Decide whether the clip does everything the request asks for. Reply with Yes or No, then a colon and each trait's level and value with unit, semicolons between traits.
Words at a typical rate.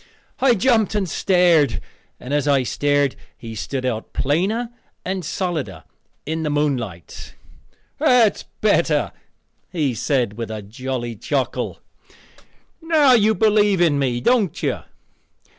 No: slow, 125 wpm